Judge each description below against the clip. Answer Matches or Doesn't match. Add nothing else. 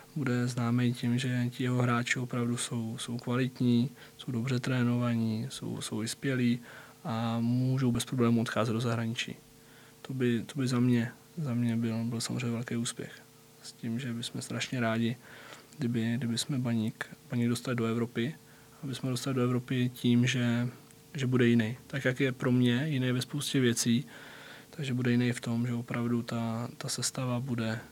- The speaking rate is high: Matches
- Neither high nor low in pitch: Doesn't match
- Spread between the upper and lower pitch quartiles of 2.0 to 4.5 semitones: Doesn't match